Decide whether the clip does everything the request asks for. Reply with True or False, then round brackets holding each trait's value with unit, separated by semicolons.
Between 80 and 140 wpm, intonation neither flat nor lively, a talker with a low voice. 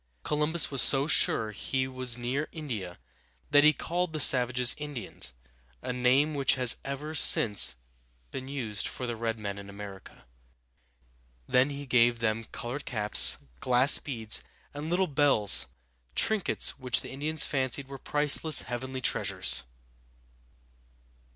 True (135 wpm; 3.9 semitones; 130 Hz)